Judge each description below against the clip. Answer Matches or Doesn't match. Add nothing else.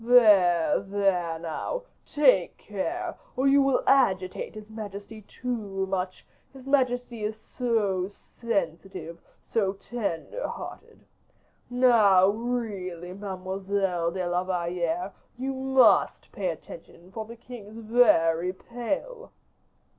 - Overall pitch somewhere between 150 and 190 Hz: Doesn't match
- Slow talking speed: Matches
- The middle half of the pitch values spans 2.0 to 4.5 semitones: Doesn't match